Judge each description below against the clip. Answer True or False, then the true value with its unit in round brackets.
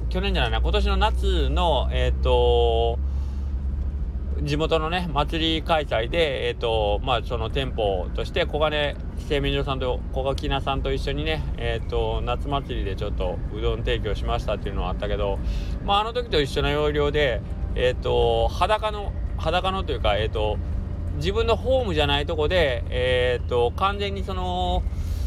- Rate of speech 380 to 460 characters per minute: False (330 characters per minute)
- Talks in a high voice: False (100 Hz)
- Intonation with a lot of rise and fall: True (7.9 semitones)